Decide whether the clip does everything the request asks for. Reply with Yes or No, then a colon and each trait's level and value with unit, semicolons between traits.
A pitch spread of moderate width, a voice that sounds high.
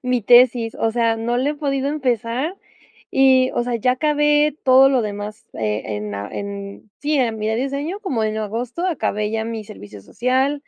Yes: average, 4.2 semitones; high, 240 Hz